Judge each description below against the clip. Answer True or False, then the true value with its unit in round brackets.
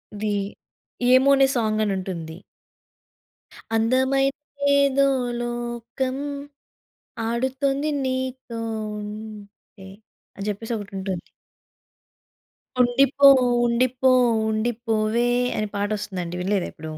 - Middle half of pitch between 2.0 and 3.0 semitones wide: False (4.0 semitones)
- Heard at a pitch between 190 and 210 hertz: False (235 Hz)